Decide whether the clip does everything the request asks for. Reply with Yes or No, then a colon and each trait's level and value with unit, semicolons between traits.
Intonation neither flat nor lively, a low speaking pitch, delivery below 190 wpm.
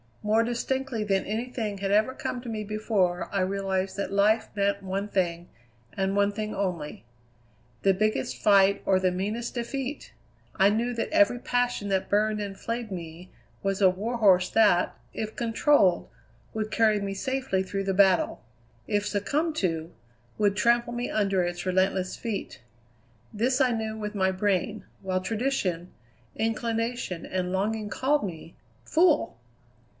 No: average, 3.2 semitones; high, 205 Hz; average, 150 wpm